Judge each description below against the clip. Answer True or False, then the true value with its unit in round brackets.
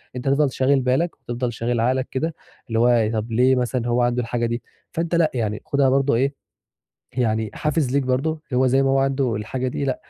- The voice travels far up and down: False (2.4 semitones)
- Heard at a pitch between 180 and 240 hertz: False (130 Hz)